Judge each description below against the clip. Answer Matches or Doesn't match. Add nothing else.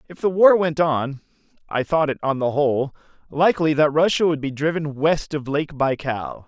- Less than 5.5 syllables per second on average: Matches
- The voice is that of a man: Matches